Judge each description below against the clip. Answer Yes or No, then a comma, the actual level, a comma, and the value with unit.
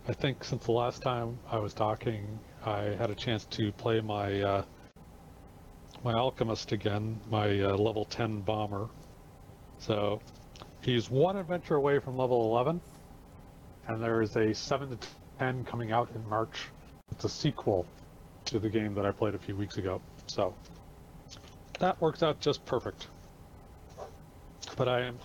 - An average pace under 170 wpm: Yes, average, 155 wpm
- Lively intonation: No, average, 3.5 semitones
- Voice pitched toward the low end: Yes, low, 115 Hz